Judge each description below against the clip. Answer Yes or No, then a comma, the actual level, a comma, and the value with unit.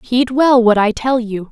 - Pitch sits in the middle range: No, high, 240 Hz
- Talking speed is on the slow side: No, fast, 235 wpm